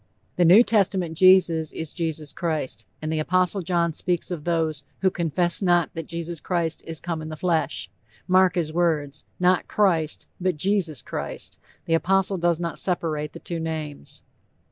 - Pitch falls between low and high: Yes, medium, 170 Hz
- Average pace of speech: Yes, average, 165 wpm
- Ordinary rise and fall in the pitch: No, narrow, 2.3 semitones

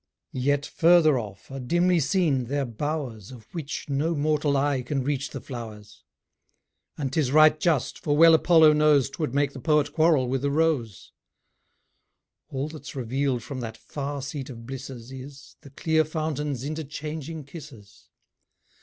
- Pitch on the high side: No, medium, 140 Hz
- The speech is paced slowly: No, average, 155 wpm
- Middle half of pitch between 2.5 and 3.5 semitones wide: Yes, average, 3.0 semitones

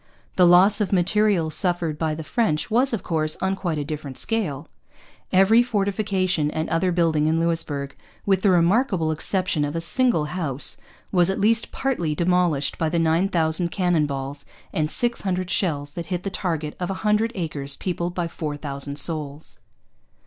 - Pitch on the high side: No, medium, 170 Hz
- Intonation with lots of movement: No, average, 3.8 semitones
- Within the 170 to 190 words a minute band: Yes, average, 175 wpm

